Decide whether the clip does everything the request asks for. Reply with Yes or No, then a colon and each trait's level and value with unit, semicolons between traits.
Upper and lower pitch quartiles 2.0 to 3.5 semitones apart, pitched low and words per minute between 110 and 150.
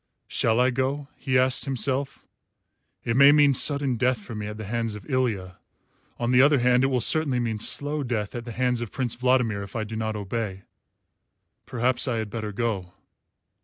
No: average, 3.1 semitones; low, 120 Hz; average, 195 wpm